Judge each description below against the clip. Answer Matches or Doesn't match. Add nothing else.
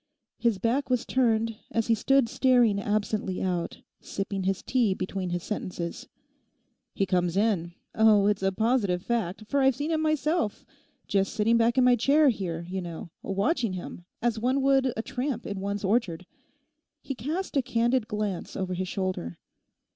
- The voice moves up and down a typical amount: Matches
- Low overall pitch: Doesn't match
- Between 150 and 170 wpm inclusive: Matches